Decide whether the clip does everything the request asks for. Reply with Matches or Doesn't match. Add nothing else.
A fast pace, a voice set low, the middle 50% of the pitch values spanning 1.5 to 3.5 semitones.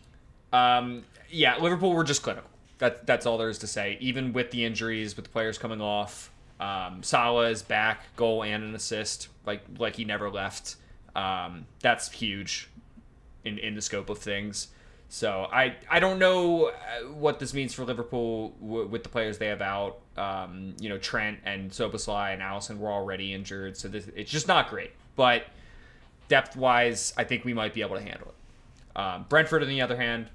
Doesn't match